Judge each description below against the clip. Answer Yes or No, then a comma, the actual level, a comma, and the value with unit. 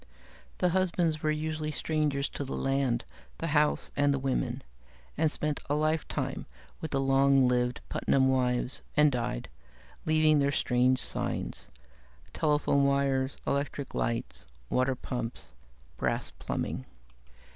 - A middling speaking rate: No, slow, 125 wpm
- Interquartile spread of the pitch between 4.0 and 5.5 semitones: No, average, 2.9 semitones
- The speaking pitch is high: No, medium, 140 Hz